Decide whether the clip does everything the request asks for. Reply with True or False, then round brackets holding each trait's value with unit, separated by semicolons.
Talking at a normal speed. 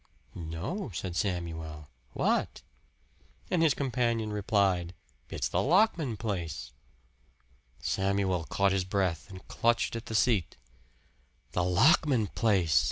False (110 wpm)